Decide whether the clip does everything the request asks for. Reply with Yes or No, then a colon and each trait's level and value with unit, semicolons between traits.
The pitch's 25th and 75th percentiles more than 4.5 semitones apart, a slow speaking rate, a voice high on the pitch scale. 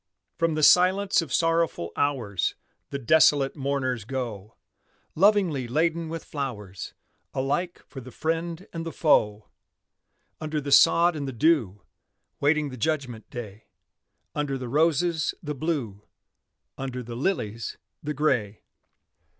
No: average, 5.2 semitones; slow, 125 wpm; medium, 140 Hz